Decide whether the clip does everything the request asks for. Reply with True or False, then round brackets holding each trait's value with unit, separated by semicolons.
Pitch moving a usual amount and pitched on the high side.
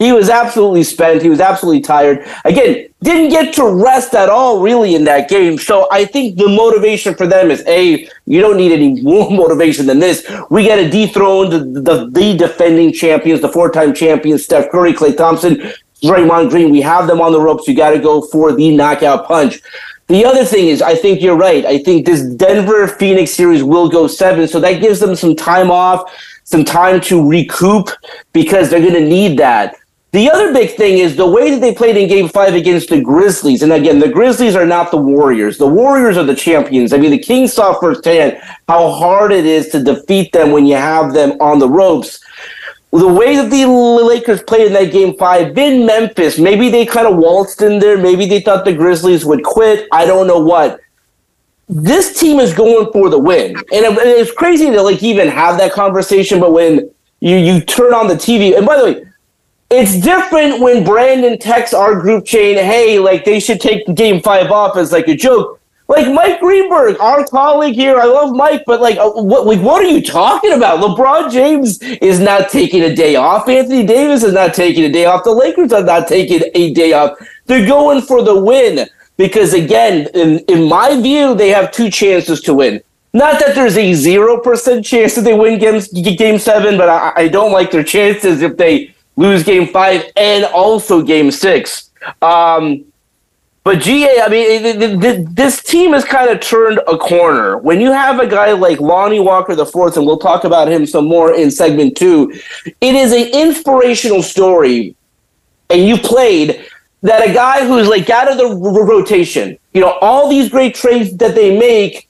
False (6.0 semitones; 200 Hz)